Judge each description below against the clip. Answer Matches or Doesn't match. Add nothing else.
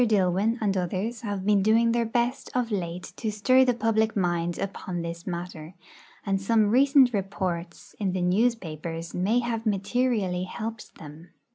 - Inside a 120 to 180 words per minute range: Matches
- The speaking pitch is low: Doesn't match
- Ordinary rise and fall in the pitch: Matches